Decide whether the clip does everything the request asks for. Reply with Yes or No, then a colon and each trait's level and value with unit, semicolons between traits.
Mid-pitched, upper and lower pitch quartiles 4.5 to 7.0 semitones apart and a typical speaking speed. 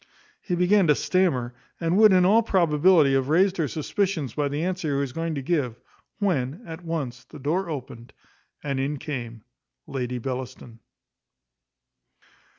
Yes: medium, 150 Hz; average, 5.3 semitones; average, 155 wpm